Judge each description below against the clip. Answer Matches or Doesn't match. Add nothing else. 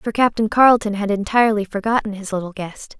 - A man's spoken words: Doesn't match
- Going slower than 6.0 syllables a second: Doesn't match